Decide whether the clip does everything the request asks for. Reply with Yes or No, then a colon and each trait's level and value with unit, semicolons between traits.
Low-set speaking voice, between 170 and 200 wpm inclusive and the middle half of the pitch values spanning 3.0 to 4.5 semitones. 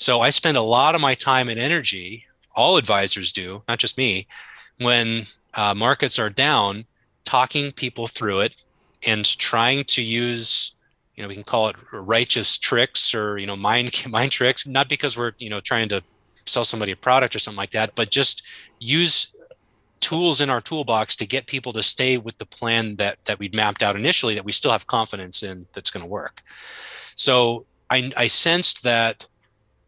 Yes: low, 115 Hz; average, 185 wpm; average, 3.5 semitones